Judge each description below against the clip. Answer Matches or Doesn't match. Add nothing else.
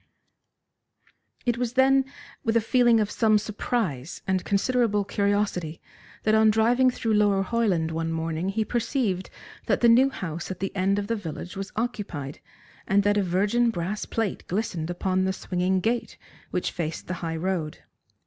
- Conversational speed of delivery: Matches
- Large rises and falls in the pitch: Doesn't match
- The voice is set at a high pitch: Matches